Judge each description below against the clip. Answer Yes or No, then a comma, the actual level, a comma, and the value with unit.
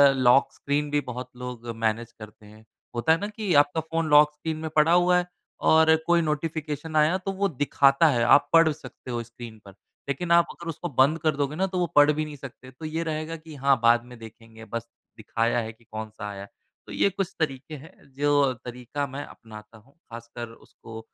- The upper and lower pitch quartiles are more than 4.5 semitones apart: Yes, average, 5.2 semitones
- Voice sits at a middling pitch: Yes, medium, 145 Hz